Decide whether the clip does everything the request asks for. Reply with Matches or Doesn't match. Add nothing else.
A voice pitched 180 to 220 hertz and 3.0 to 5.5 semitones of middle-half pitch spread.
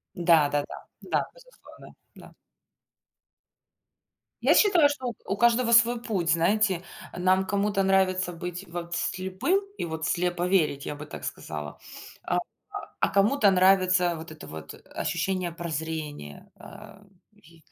Matches